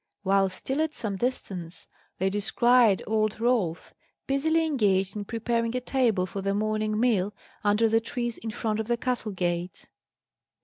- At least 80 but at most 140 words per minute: No, average, 160 wpm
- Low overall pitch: No, high, 215 Hz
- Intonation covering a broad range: No, average, 3.6 semitones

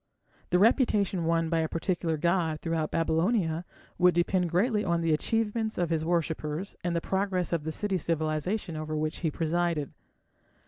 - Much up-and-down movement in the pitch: No, narrow, 2.6 semitones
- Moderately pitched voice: Yes, medium, 170 Hz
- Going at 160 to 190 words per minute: Yes, average, 165 wpm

